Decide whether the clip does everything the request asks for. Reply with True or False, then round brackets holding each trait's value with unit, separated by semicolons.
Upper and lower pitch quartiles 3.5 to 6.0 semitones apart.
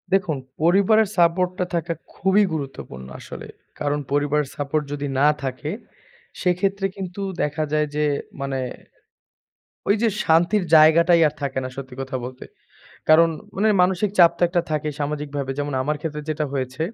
True (3.8 semitones)